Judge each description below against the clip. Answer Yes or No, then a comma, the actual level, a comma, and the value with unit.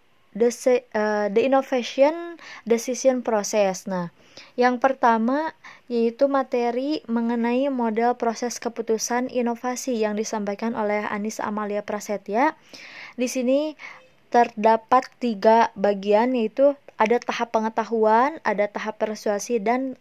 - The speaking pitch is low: No, high, 235 Hz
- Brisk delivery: No, average, 105 wpm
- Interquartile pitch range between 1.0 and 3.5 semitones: Yes, average, 2.7 semitones